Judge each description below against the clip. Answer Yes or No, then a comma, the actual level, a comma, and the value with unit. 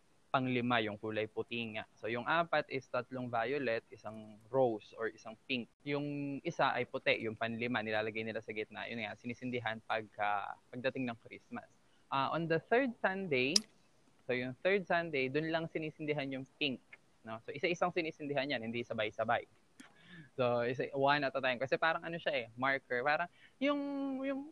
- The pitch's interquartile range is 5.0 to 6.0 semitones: Yes, wide, 5.6 semitones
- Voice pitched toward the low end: Yes, low, 130 Hz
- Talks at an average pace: No, fast, 170 wpm